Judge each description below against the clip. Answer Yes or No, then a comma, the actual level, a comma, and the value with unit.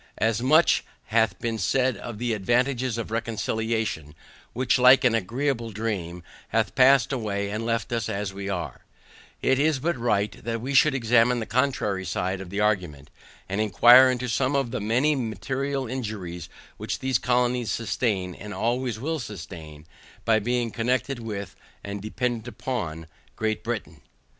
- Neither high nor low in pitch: No, low, 115 Hz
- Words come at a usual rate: Yes, average, 155 wpm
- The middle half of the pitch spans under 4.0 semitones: Yes, average, 3.6 semitones